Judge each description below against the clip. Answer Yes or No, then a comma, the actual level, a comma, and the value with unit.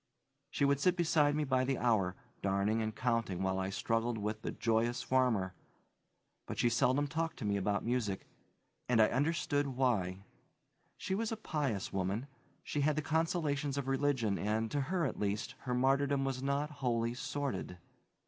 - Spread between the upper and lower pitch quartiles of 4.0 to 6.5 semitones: Yes, average, 4.9 semitones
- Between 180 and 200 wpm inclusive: No, average, 170 wpm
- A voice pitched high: No, low, 130 Hz